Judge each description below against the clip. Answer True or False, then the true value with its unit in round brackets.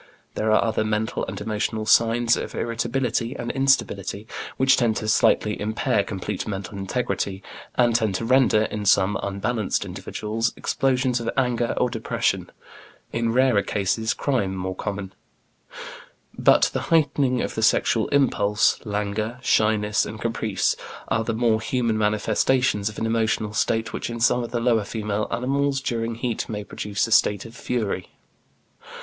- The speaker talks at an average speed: True (150 wpm)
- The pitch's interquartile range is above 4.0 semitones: False (2.5 semitones)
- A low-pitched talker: True (110 Hz)